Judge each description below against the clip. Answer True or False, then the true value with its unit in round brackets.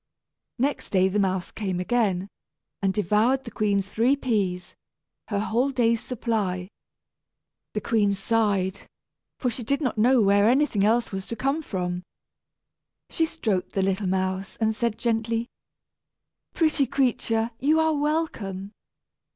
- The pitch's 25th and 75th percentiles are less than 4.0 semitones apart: False (4.3 semitones)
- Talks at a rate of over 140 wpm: False (135 wpm)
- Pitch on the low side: False (220 Hz)